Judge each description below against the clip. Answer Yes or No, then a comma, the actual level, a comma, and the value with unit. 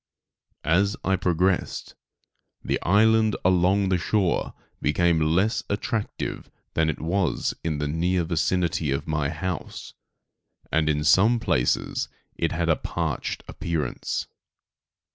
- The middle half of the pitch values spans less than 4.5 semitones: Yes, average, 3.4 semitones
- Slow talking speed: Yes, slow, 120 wpm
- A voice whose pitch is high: No, very low, 85 Hz